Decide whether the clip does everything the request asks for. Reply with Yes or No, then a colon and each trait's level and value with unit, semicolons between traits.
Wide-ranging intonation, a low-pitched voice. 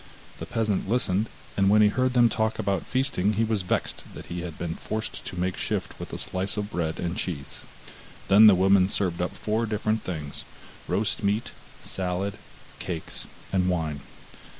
No: average, 3.3 semitones; low, 100 Hz